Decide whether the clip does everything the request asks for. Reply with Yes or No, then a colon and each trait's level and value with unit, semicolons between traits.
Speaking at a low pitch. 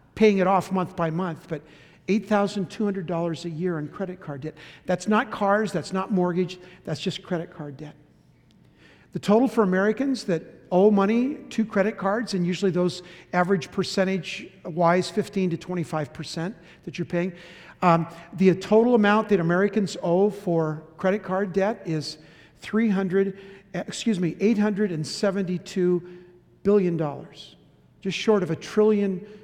No: medium, 185 Hz